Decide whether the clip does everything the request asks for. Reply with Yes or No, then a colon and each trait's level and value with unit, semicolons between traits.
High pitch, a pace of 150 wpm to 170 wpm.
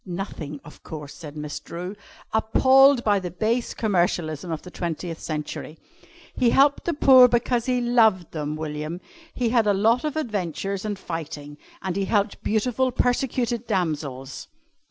Yes: high, 195 Hz; average, 155 wpm